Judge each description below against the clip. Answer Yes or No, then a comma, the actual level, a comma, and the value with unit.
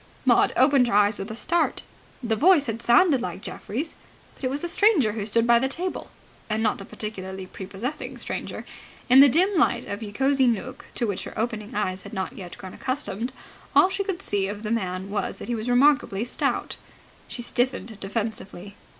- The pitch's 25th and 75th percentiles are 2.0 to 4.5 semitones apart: No, average, 4.9 semitones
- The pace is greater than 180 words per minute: Yes, average, 200 wpm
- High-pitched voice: Yes, high, 230 Hz